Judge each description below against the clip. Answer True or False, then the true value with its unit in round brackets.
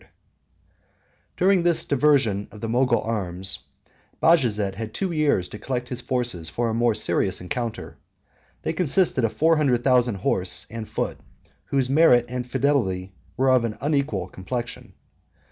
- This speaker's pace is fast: False (155 wpm)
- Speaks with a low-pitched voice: True (120 Hz)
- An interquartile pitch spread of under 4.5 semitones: False (4.9 semitones)